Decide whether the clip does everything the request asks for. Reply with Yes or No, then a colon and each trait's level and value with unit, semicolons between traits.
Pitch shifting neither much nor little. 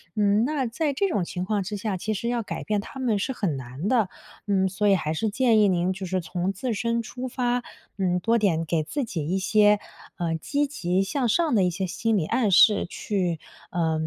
Yes: average, 4.5 semitones